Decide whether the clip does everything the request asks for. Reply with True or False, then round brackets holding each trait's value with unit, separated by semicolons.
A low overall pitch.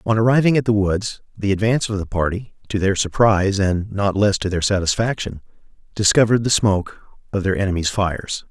True (100 Hz)